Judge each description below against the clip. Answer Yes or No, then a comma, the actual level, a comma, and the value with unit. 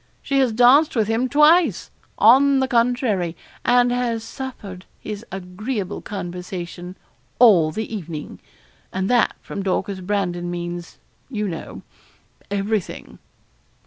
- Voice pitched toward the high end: Yes, high, 210 Hz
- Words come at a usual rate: No, slow, 115 wpm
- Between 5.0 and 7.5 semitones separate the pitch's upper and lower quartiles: Yes, wide, 5.4 semitones